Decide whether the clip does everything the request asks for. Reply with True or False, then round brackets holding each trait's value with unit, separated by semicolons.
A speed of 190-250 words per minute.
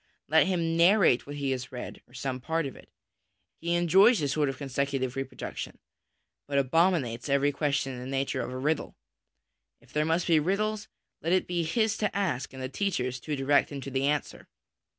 True (200 wpm)